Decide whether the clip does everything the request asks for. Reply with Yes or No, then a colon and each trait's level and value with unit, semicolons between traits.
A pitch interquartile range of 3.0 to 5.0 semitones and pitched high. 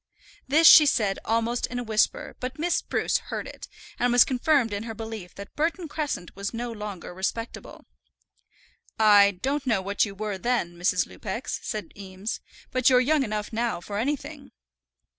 Yes: average, 4.0 semitones; high, 225 Hz